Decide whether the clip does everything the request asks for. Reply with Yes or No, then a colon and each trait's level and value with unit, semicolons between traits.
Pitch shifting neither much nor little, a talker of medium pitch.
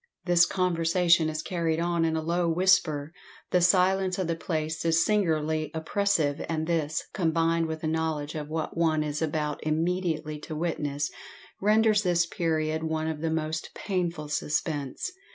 No: narrow, 2.0 semitones; medium, 160 Hz